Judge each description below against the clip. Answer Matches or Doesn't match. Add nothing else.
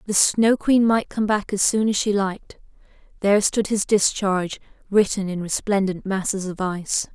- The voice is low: Doesn't match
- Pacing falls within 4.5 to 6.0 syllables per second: Matches